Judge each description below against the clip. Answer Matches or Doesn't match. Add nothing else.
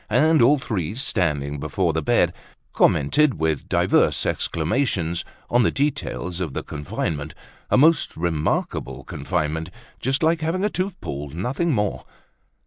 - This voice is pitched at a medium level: Doesn't match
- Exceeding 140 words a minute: Doesn't match